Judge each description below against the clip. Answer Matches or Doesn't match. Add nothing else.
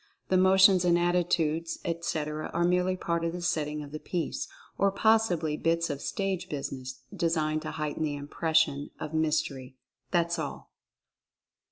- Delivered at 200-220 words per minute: Doesn't match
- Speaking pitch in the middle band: Matches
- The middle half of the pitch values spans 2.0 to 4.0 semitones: Matches